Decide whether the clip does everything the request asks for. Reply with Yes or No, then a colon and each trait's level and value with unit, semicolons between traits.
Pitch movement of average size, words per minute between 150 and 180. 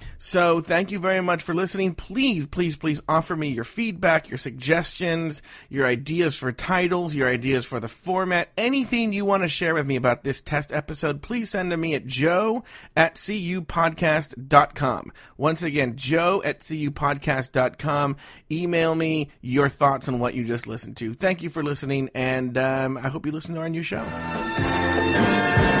Yes: average, 4.7 semitones; average, 170 wpm